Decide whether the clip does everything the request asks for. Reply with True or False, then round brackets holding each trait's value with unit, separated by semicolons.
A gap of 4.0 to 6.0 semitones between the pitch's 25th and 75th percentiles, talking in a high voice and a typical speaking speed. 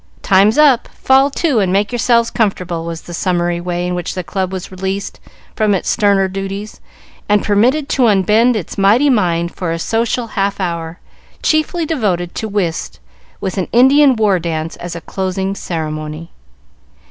True (4.7 semitones; 195 Hz; 165 wpm)